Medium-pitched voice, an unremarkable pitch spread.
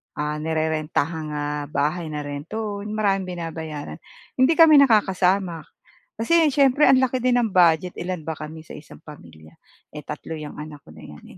No: medium, 165 Hz; wide, 5.9 semitones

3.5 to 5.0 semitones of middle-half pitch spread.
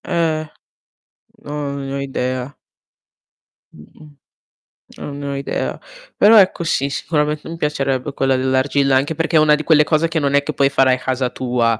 No: narrow, 2.5 semitones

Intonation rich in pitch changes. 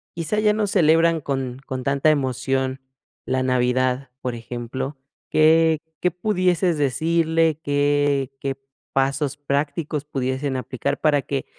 No: average, 3.5 semitones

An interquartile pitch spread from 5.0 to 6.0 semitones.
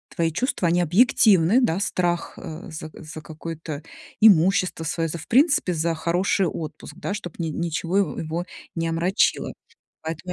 No: average, 2.7 semitones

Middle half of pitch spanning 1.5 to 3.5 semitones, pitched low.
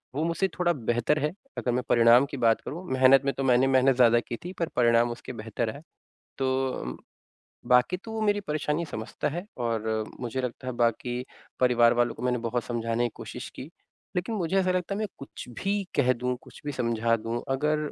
No: average, 4.1 semitones; low, 125 Hz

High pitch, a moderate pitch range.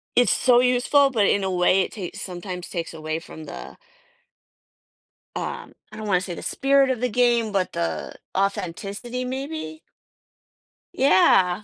No: high, 200 Hz; wide, 5.7 semitones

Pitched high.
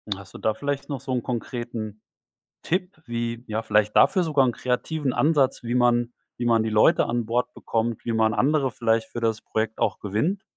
No: low, 120 Hz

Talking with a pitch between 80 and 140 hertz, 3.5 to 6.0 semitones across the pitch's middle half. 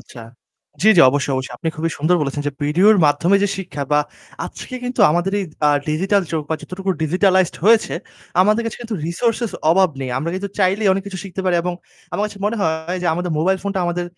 No: medium, 185 Hz; average, 3.9 semitones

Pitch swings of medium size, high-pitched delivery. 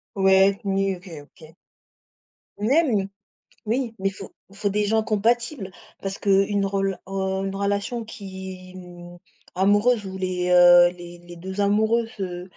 No: narrow, 1.9 semitones; high, 195 Hz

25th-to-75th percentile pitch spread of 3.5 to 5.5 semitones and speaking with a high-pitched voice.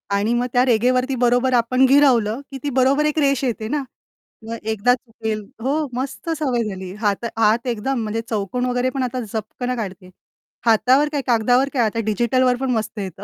No: average, 2.9 semitones; high, 245 Hz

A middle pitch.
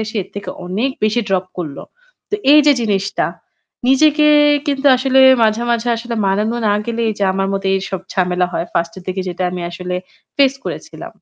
No: high, 205 Hz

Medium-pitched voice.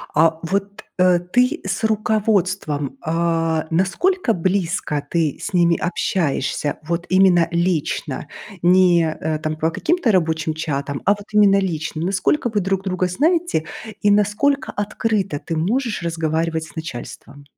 Yes: medium, 180 Hz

